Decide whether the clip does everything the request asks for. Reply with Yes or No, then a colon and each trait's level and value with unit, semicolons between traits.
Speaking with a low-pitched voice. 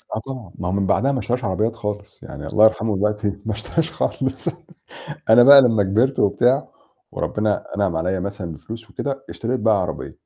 Yes: low, 110 Hz